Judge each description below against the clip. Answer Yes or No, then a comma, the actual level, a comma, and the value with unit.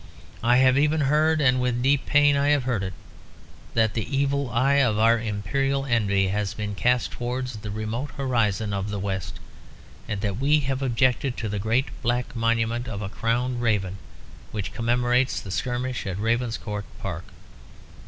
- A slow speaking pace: No, average, 170 wpm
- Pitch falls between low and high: No, low, 120 Hz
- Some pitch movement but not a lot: Yes, average, 3.8 semitones